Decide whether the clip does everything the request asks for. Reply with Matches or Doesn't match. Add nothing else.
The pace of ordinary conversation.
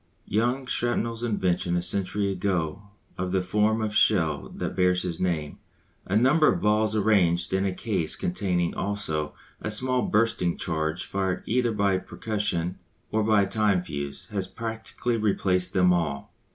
Matches